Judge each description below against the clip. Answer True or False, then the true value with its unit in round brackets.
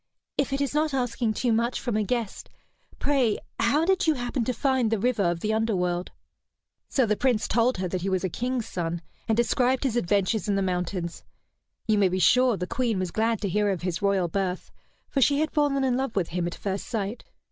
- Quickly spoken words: True (225 wpm)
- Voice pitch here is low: False (220 Hz)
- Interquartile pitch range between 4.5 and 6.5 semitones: True (5.0 semitones)